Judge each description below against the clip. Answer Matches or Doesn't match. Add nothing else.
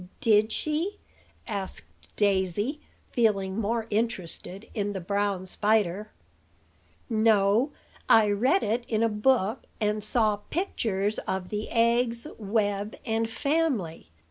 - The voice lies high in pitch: Matches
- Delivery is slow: Matches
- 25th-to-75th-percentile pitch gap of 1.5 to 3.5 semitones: Matches